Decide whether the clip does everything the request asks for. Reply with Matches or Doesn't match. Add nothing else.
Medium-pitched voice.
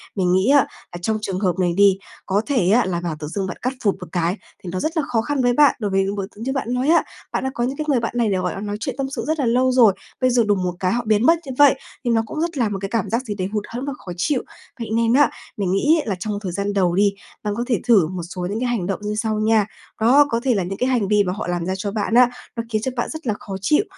Doesn't match